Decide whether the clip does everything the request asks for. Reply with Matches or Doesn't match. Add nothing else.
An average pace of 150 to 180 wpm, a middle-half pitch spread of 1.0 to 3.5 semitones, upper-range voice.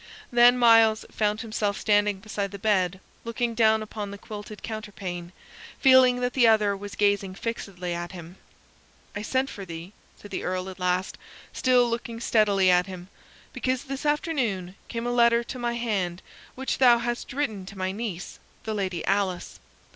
Doesn't match